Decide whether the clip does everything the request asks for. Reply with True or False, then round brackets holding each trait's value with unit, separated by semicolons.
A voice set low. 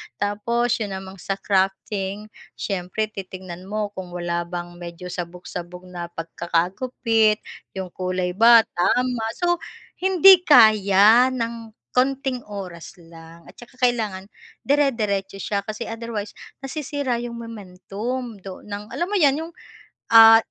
False (205 Hz)